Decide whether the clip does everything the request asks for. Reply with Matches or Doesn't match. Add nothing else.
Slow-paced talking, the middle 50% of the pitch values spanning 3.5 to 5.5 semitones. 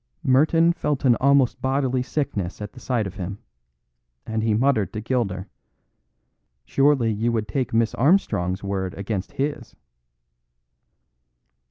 Matches